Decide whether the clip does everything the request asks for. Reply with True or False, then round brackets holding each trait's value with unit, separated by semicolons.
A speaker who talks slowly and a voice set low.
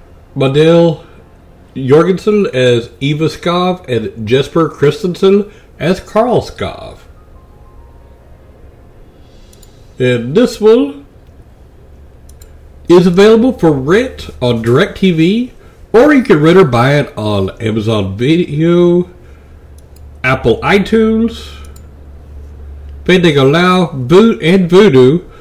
True (85 wpm; 130 Hz)